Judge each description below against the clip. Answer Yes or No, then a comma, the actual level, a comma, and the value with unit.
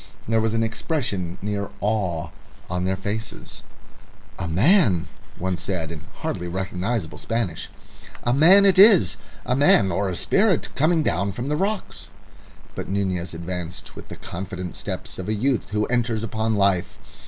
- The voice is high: No, low, 100 Hz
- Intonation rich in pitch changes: No, average, 5.0 semitones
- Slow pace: No, average, 155 wpm